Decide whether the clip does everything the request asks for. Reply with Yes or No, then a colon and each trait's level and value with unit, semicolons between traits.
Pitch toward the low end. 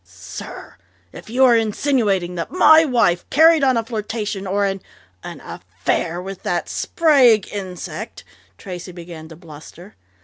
No: high, 205 Hz